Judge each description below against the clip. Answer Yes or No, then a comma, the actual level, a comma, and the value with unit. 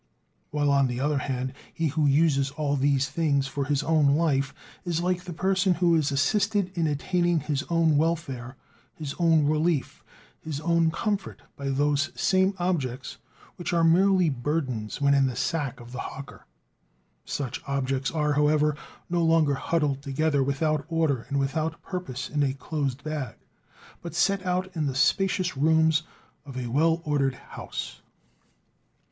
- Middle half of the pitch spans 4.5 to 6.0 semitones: No, average, 3.3 semitones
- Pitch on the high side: No, medium, 150 Hz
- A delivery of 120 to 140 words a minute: No, average, 160 wpm